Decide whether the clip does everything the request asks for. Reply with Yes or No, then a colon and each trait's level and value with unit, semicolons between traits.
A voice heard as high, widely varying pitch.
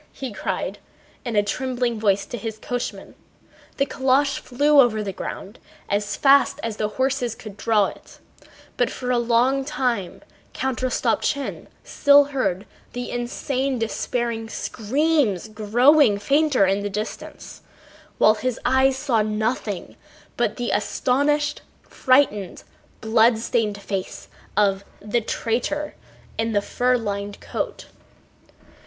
No: high, 235 Hz; average, 4.0 semitones